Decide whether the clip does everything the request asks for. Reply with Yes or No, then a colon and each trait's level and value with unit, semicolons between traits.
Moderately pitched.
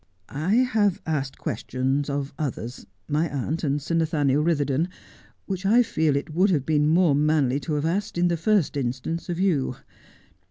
Yes: medium, 155 Hz